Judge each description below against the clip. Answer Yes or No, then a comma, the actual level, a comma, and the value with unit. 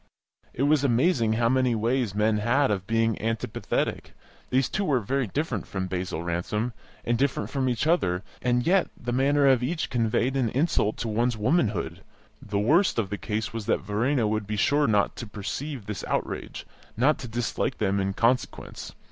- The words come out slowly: No, average, 180 wpm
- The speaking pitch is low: Yes, low, 115 Hz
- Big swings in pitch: No, average, 4.1 semitones